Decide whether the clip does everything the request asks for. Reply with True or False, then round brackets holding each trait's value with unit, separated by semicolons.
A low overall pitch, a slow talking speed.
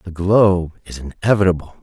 True (90 Hz; 130 wpm)